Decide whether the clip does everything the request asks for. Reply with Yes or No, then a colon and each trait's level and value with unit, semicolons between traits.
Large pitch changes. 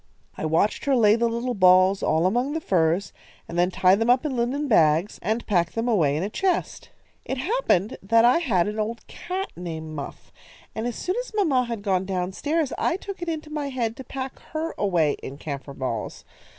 Yes: wide, 7.0 semitones